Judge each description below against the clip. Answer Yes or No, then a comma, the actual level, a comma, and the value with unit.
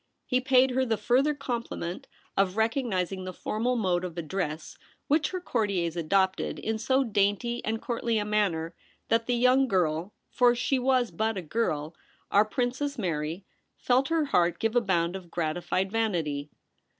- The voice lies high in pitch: Yes, high, 215 Hz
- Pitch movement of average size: No, wide, 5.8 semitones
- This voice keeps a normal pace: Yes, average, 170 wpm